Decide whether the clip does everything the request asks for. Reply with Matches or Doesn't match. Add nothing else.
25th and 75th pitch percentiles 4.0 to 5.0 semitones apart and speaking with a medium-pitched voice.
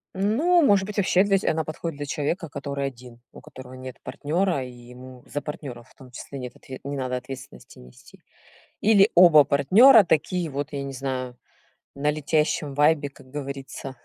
Matches